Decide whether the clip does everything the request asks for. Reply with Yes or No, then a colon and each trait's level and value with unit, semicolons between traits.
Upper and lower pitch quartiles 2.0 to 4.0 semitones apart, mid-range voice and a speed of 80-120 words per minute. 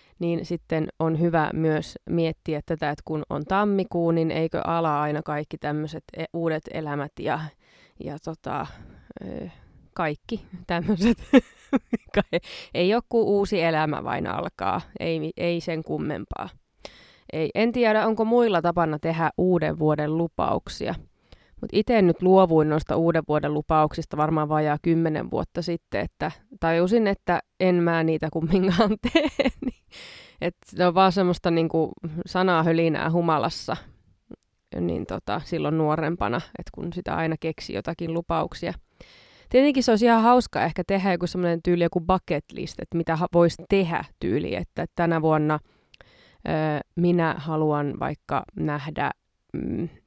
No: average, 2.7 semitones; medium, 165 Hz; average, 135 wpm